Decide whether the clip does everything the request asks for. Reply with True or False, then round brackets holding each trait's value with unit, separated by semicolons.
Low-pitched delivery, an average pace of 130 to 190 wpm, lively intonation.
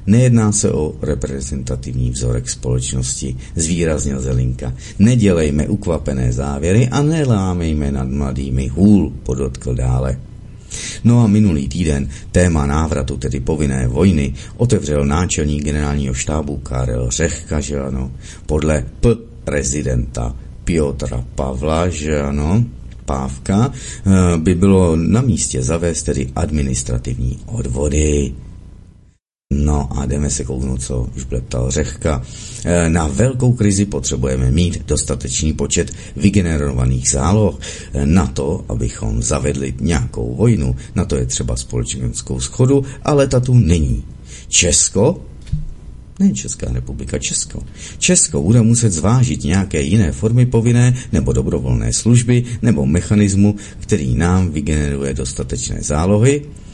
False (75 Hz; 115 wpm; 7.5 semitones)